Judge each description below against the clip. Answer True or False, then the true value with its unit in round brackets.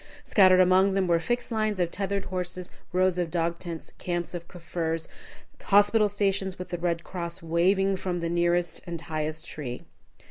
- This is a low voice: False (175 Hz)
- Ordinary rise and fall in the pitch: False (2.2 semitones)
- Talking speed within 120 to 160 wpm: False (170 wpm)